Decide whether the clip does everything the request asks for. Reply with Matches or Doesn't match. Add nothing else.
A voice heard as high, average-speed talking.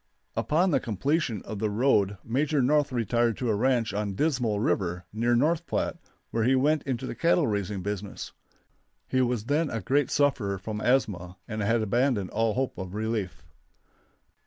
Doesn't match